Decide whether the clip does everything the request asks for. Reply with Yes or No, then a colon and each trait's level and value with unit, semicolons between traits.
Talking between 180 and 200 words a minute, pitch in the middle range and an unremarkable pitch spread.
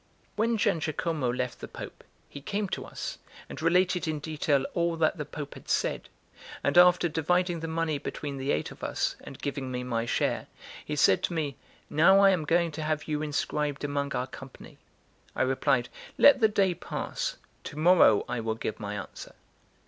Yes: average, 185 wpm; medium, 155 Hz; average, 4.2 semitones